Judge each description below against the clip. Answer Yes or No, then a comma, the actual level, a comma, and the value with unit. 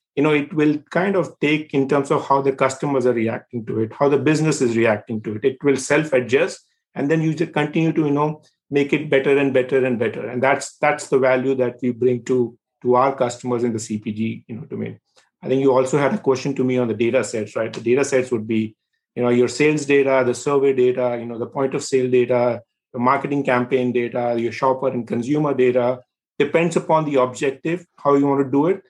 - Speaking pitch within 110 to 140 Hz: Yes, low, 135 Hz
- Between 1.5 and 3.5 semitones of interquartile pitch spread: Yes, average, 2.8 semitones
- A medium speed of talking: No, fast, 235 wpm